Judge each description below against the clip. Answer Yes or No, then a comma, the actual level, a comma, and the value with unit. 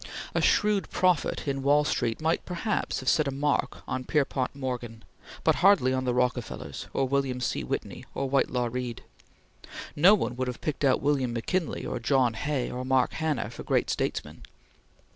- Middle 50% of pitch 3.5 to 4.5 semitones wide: No, average, 2.9 semitones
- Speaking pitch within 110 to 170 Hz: Yes, low, 135 Hz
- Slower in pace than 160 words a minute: No, average, 175 wpm